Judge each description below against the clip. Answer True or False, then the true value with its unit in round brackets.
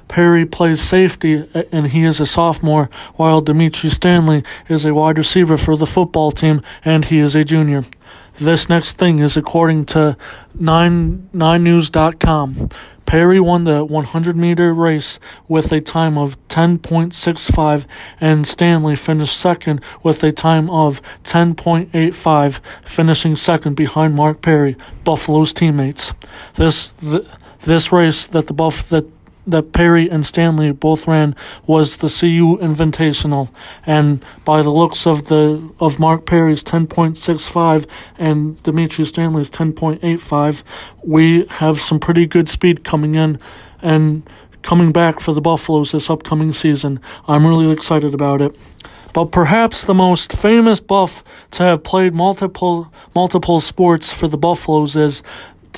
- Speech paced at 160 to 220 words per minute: False (140 wpm)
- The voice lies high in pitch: False (160 Hz)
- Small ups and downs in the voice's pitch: True (1.7 semitones)